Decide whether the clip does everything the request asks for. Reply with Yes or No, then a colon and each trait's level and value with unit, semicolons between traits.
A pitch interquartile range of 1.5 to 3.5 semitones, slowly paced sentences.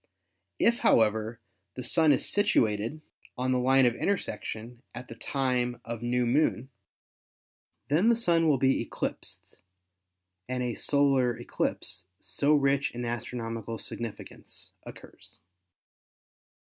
Yes: average, 3.2 semitones; slow, 120 wpm